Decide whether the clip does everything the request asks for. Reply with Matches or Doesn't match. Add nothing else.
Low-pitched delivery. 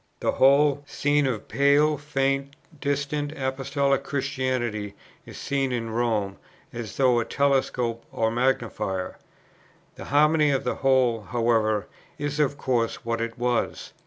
Matches